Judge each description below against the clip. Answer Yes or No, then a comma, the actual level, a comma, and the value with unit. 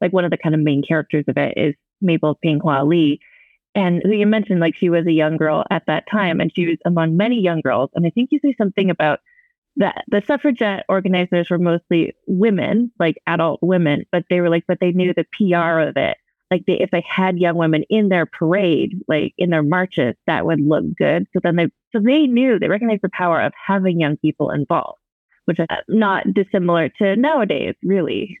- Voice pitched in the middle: Yes, medium, 180 Hz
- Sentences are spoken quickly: Yes, fast, 215 wpm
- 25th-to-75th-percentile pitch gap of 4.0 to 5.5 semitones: No, average, 3.6 semitones